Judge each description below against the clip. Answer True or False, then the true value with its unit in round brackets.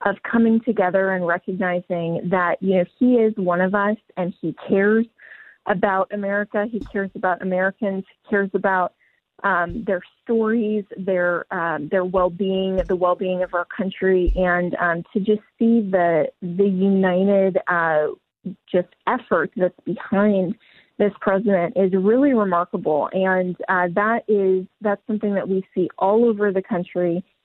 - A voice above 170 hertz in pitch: True (190 Hz)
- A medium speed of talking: True (150 wpm)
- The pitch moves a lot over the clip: False (2.4 semitones)